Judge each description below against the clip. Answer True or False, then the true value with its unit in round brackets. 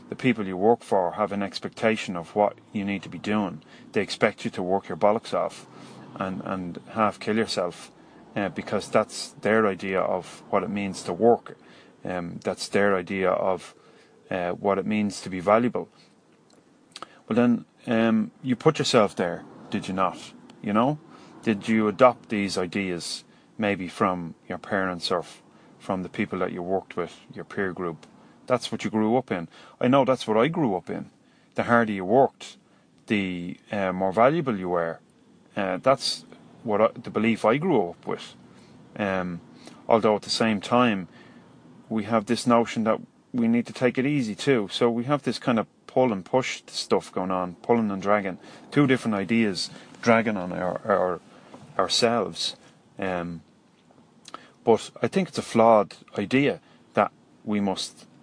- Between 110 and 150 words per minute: False (175 wpm)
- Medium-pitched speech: False (105 Hz)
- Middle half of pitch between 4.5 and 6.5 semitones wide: False (3.8 semitones)